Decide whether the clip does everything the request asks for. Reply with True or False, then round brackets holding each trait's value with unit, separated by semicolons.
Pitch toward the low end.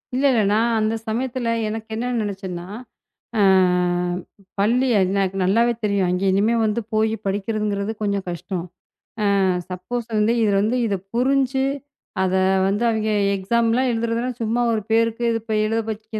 False (220 Hz)